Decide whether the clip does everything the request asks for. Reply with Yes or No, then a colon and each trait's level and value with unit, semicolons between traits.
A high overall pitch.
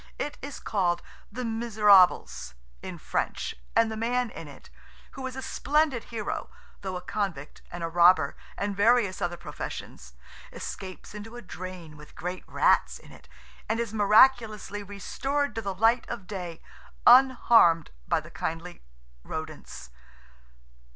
Yes: high, 205 Hz